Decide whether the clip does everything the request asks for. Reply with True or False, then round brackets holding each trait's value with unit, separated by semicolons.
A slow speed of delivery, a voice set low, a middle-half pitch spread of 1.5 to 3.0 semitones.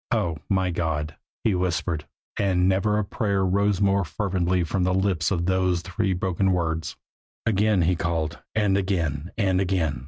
False (155 wpm; 95 Hz; 2.5 semitones)